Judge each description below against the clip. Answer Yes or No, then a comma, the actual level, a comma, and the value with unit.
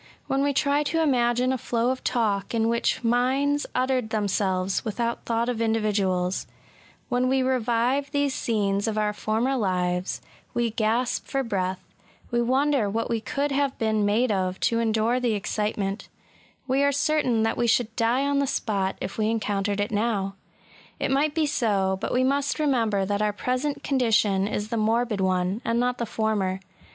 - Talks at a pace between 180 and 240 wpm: Yes, average, 185 wpm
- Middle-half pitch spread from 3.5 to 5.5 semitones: Yes, average, 3.8 semitones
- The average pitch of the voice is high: Yes, high, 230 Hz